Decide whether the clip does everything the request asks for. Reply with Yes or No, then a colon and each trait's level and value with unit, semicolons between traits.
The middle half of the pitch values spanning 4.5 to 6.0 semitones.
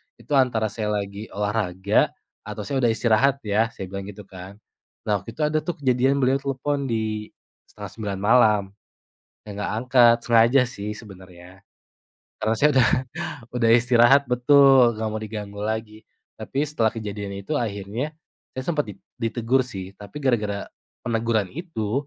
No: average, 3.8 semitones